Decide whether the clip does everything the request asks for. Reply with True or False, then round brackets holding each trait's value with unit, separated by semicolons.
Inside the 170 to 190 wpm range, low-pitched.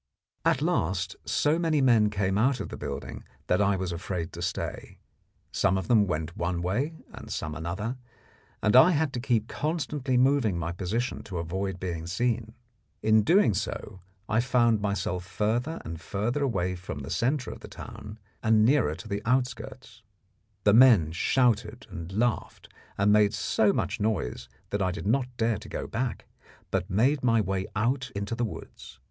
True (175 wpm; 110 Hz)